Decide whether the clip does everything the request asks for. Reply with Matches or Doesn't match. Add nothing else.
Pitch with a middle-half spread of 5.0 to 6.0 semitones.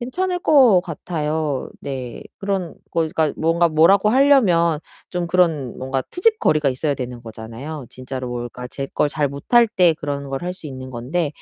Matches